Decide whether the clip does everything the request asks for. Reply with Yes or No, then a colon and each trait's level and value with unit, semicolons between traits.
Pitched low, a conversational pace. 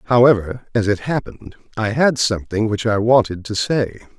Yes: low, 110 Hz; average, 170 wpm